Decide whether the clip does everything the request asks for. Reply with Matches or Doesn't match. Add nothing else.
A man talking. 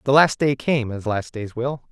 Matches